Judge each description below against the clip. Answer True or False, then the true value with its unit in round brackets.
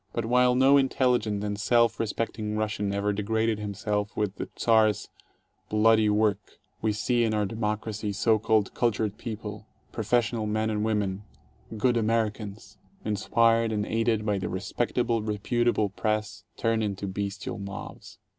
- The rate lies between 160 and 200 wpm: False (145 wpm)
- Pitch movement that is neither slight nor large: False (1.7 semitones)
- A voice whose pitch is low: True (110 Hz)